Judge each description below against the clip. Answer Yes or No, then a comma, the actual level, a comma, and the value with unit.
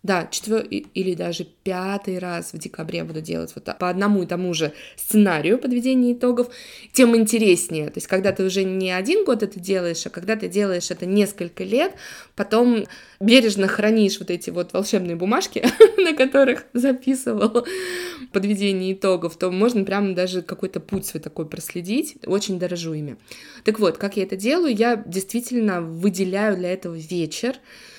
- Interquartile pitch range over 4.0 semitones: Yes, average, 4.6 semitones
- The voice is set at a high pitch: Yes, high, 195 Hz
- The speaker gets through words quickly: Yes, fast, 165 wpm